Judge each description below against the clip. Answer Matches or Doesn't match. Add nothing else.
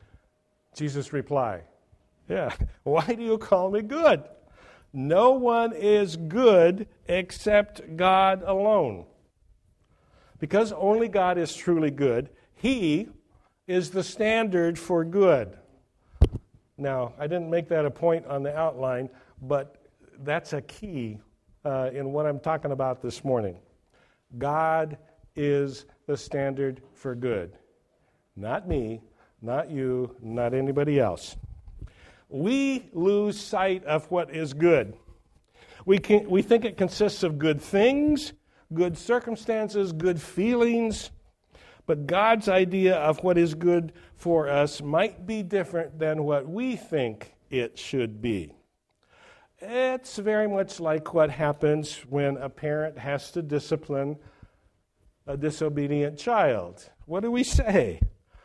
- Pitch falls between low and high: Matches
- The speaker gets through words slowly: Matches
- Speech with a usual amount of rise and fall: Doesn't match